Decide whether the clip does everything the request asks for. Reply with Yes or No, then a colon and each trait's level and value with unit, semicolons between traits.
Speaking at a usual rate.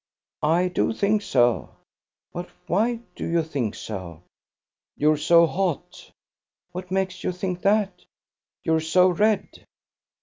No: slow, 125 wpm